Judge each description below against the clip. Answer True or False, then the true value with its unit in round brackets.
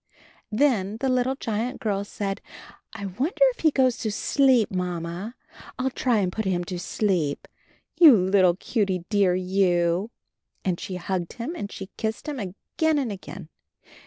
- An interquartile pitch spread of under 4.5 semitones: False (5.4 semitones)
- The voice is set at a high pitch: True (200 Hz)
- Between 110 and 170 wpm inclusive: True (160 wpm)